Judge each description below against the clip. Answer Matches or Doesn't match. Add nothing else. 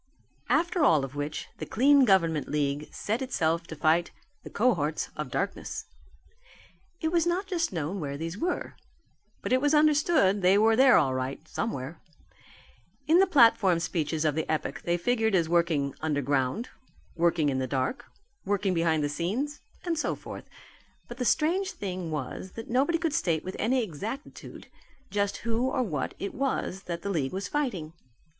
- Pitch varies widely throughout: Matches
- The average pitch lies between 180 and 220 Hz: Matches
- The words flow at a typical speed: Matches